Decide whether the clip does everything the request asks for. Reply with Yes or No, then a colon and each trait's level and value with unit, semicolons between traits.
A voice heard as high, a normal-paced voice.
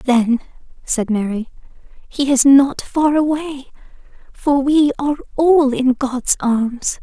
No: very high, 270 Hz; slow, 130 wpm